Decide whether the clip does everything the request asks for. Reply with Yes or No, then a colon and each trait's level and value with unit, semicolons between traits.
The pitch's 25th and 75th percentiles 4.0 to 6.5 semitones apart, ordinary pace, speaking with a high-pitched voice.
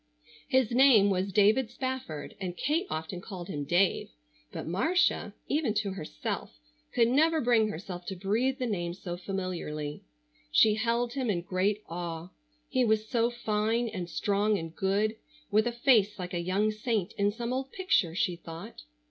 Yes: average, 4.9 semitones; average, 165 wpm; high, 210 Hz